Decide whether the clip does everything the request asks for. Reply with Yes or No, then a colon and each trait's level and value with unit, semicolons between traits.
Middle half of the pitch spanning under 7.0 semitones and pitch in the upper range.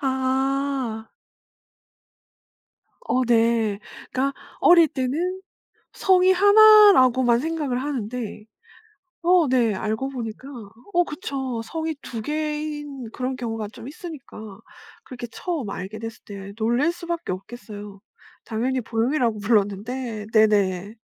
Yes: average, 5.2 semitones; very high, 255 Hz